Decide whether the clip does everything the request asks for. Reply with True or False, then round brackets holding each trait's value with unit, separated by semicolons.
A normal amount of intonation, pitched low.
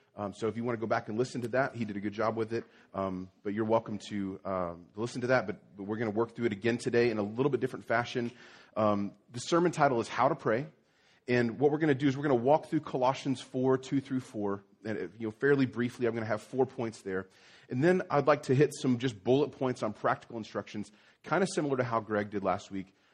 True (3.9 semitones; 115 Hz)